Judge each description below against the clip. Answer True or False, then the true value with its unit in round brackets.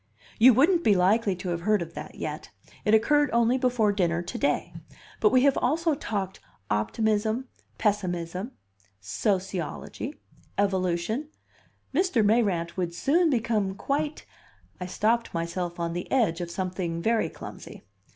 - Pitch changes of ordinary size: False (5.8 semitones)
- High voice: True (210 Hz)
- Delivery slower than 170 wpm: True (140 wpm)